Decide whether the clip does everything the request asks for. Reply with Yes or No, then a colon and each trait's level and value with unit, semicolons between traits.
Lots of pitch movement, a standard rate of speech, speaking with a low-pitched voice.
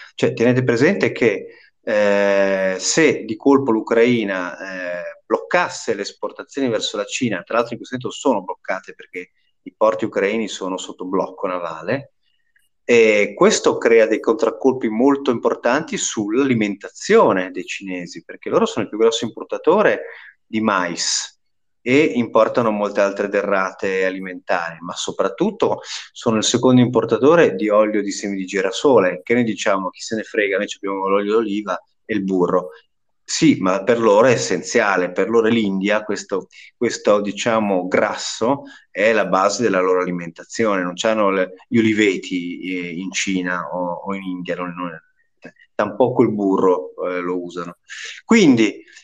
Yes: wide, 6.8 semitones; average, 150 wpm; low, 110 Hz